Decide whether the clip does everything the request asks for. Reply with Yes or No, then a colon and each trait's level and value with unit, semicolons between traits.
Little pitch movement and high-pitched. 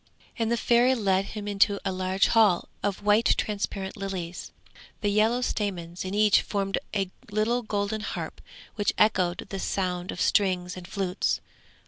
Yes: narrow, 2.3 semitones; high, 200 Hz